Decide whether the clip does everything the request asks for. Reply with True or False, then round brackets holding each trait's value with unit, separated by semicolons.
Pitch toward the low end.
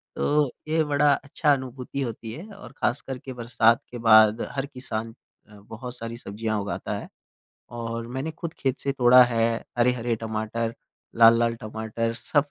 True (120 Hz)